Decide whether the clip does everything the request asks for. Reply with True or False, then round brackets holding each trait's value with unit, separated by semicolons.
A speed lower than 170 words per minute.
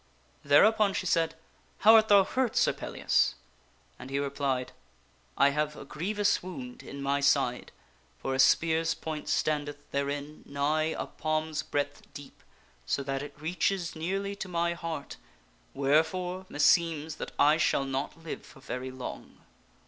True (155 wpm)